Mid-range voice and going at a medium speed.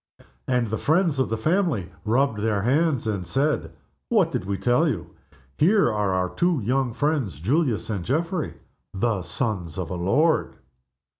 No: low, 120 Hz; average, 160 wpm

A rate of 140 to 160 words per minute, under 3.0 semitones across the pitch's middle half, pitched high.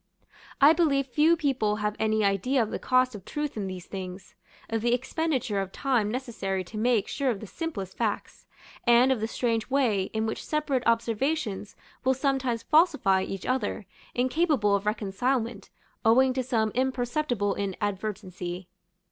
No: average, 155 wpm; average, 4.4 semitones; high, 230 Hz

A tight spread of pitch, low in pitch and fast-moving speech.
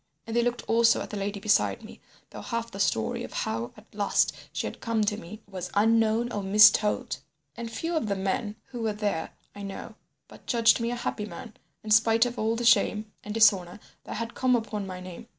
No: narrow, 2.3 semitones; high, 215 Hz; fast, 220 wpm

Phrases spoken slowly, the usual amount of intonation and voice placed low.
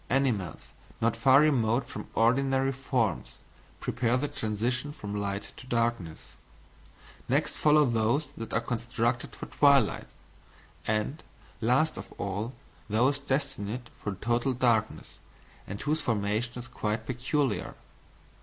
Yes: slow, 120 wpm; average, 3.6 semitones; low, 120 Hz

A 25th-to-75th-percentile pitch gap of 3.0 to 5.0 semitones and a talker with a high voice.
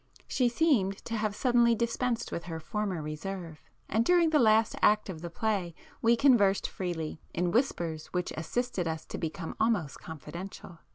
No: wide, 5.6 semitones; high, 195 Hz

